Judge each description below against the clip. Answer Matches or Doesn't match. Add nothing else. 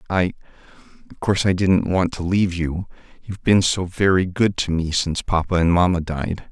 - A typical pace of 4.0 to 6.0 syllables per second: Matches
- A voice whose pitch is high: Doesn't match